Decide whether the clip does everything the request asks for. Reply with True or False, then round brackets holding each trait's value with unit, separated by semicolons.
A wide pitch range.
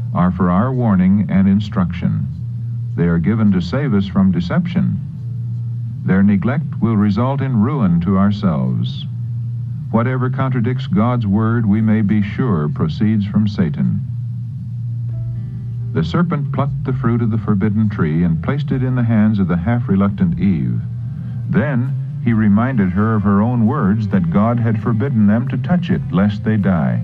False (3.8 semitones)